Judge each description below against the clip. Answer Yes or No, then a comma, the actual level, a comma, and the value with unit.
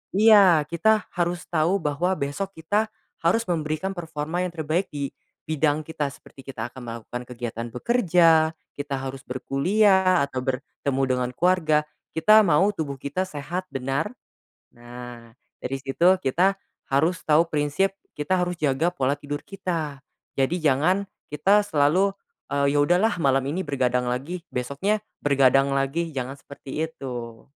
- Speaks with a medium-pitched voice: Yes, medium, 150 Hz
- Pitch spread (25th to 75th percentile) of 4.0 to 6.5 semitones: Yes, average, 4.9 semitones